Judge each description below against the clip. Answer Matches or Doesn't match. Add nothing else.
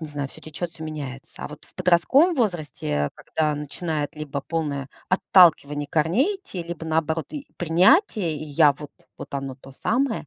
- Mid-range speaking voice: Matches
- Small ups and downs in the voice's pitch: Doesn't match